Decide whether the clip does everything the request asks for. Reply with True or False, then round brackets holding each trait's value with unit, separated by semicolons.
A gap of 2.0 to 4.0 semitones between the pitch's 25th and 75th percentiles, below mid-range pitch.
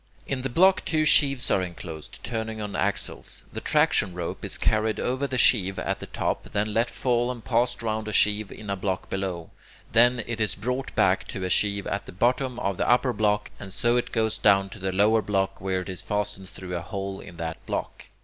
True (3.7 semitones; 105 Hz)